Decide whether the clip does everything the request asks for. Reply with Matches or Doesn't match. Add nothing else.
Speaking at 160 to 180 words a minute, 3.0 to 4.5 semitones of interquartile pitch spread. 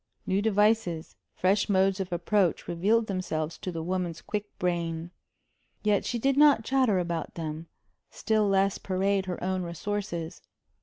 Doesn't match